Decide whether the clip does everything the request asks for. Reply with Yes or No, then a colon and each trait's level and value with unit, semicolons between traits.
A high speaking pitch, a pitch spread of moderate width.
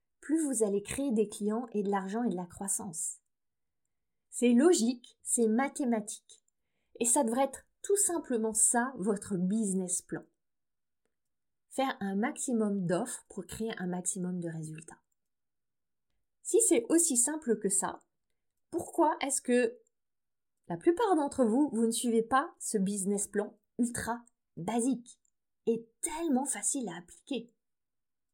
Yes: high, 235 Hz; average, 4.8 semitones